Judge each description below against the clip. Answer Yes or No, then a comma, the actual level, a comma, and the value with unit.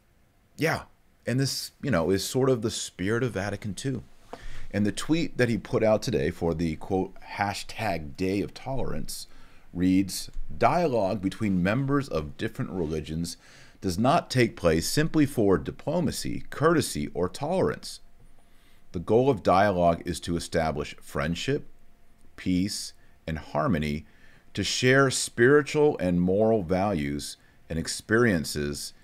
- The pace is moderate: No, slow, 130 wpm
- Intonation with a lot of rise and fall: Yes, wide, 5.9 semitones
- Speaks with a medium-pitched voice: No, very low, 95 Hz